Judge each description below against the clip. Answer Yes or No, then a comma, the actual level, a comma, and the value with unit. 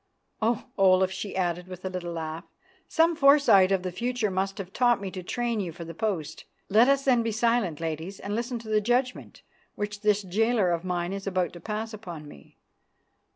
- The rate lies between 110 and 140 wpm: No, average, 200 wpm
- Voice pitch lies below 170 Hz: No, high, 195 Hz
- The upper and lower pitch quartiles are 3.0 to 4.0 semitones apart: No, average, 4.4 semitones